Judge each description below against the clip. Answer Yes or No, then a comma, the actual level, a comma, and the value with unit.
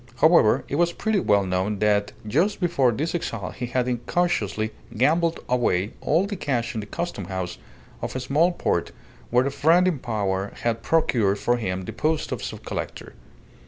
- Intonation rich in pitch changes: Yes, wide, 7.9 semitones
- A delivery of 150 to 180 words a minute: Yes, average, 175 wpm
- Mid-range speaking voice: No, low, 125 Hz